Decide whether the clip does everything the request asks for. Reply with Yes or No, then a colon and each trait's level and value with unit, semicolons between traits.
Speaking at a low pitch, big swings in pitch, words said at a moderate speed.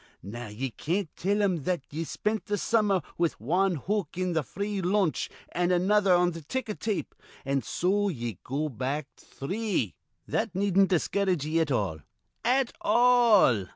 No: medium, 180 Hz; wide, 5.8 semitones; average, 160 wpm